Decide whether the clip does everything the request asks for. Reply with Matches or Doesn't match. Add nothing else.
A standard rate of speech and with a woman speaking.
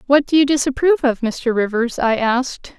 Matches